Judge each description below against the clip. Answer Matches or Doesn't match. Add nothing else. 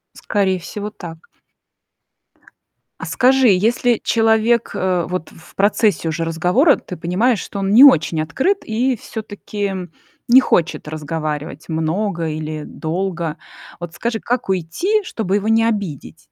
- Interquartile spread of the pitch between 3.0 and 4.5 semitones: Doesn't match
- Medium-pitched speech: Doesn't match